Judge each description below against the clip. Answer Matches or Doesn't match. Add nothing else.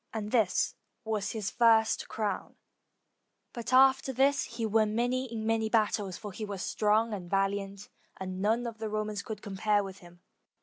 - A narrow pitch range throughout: Matches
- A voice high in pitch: Matches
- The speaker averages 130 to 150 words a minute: Doesn't match